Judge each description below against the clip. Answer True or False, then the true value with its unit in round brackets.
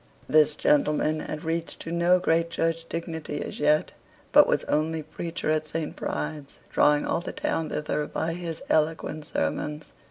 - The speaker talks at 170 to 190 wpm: False (160 wpm)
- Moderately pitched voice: True (155 Hz)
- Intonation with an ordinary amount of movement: False (1.5 semitones)